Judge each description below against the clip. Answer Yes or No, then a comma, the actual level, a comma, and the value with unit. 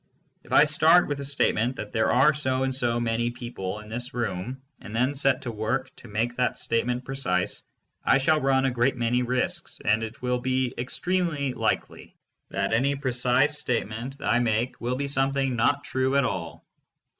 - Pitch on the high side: No, low, 125 Hz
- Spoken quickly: No, average, 185 wpm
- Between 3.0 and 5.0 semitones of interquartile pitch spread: No, narrow, 2.5 semitones